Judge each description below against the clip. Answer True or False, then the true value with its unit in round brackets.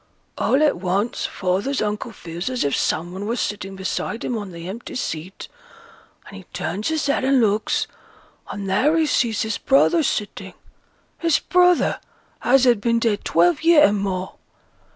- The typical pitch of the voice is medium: False (215 Hz)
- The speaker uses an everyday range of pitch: False (5.8 semitones)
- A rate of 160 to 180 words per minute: True (170 wpm)